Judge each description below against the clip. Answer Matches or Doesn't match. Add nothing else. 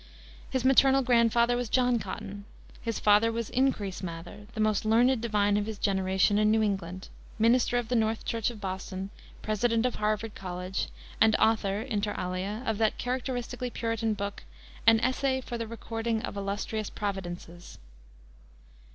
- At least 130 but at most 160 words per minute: Matches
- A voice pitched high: Matches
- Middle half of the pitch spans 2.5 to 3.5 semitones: Matches